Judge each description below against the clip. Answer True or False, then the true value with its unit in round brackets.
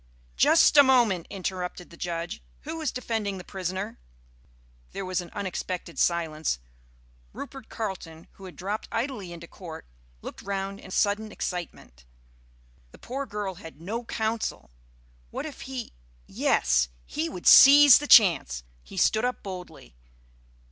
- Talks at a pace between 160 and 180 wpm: False (140 wpm)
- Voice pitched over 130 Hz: True (190 Hz)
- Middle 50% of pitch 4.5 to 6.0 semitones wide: True (4.9 semitones)